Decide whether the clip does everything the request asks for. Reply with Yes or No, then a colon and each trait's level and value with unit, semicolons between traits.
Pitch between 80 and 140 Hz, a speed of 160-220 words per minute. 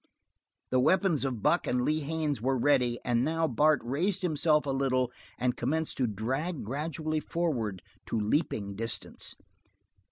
No: low, 135 Hz; average, 150 wpm